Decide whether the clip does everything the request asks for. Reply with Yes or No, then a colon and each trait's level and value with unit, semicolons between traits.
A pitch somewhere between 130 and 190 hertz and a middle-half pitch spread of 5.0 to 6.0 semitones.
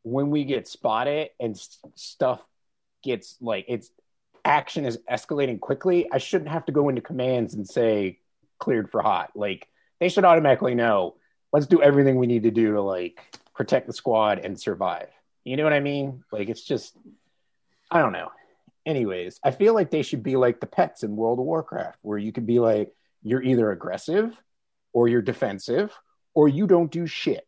Yes: low, 135 Hz; wide, 5.4 semitones